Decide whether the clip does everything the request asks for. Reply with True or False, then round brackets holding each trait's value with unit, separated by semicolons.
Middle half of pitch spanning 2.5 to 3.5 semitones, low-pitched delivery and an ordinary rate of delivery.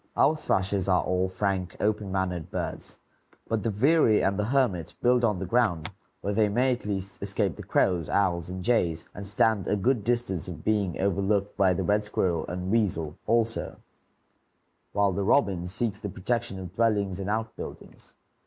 True (3.2 semitones; 100 Hz; 175 wpm)